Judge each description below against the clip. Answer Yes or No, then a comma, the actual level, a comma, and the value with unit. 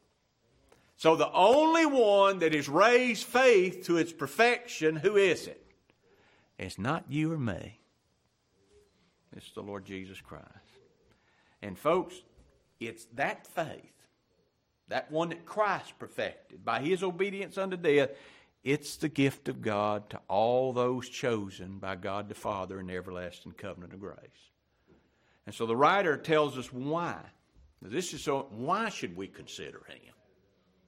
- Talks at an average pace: Yes, average, 145 wpm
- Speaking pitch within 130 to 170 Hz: Yes, medium, 140 Hz